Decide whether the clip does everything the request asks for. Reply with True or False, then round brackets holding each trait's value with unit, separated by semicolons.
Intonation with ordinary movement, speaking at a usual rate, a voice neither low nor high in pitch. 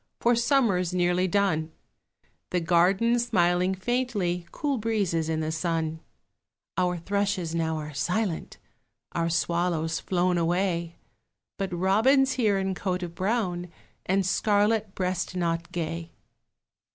False (3.2 semitones; 120 wpm; 180 Hz)